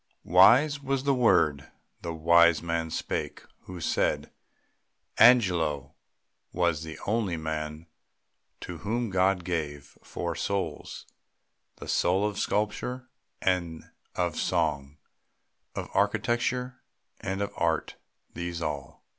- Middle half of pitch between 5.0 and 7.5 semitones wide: No, average, 4.6 semitones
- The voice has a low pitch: Yes, very low, 85 Hz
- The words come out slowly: Yes, slow, 110 wpm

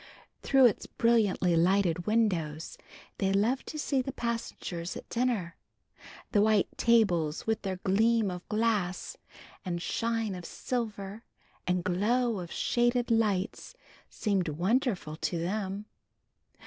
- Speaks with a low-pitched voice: No, high, 205 Hz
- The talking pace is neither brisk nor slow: No, slow, 120 wpm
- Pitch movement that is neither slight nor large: Yes, average, 4.4 semitones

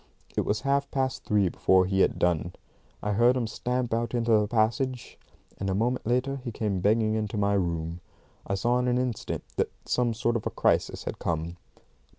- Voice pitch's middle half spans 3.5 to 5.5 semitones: Yes, average, 3.9 semitones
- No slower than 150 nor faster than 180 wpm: No, average, 195 wpm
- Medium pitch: No, low, 110 Hz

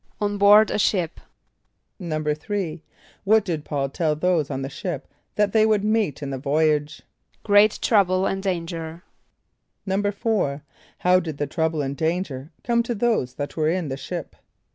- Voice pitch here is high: No, medium, 170 Hz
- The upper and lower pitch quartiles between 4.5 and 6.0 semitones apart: Yes, average, 5.2 semitones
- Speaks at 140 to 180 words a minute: Yes, average, 160 wpm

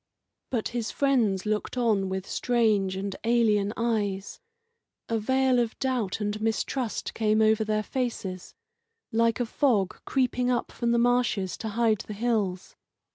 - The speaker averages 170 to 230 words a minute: No, average, 145 wpm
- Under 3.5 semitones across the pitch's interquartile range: Yes, average, 2.8 semitones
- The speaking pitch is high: Yes, high, 220 Hz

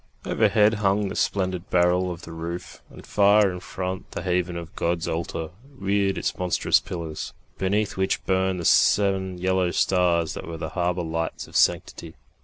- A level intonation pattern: Yes, narrow, 2.1 semitones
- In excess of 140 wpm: Yes, average, 170 wpm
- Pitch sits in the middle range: No, very low, 90 Hz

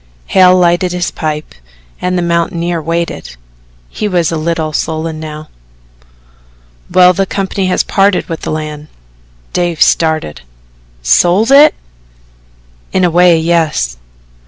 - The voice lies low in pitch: No, medium, 170 Hz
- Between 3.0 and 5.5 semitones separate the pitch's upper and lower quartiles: No, narrow, 2.4 semitones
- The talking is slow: Yes, slow, 125 wpm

